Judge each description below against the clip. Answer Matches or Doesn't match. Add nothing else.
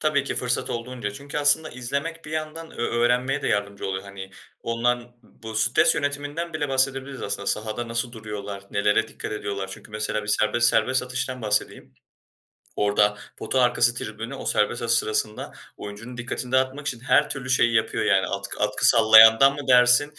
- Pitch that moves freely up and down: Doesn't match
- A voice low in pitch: Matches